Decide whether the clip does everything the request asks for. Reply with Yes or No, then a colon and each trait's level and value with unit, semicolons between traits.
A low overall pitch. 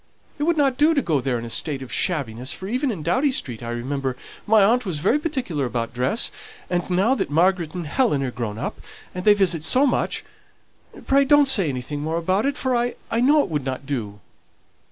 No: medium, 175 Hz